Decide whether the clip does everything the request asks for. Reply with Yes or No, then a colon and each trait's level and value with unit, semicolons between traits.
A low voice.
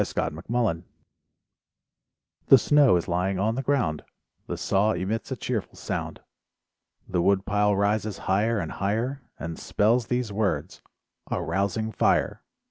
Yes: low, 105 Hz